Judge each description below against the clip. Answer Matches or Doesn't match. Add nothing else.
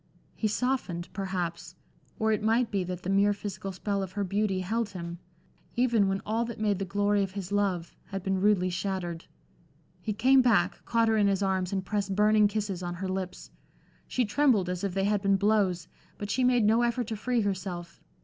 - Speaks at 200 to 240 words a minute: Matches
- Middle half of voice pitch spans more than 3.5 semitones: Doesn't match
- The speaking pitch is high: Matches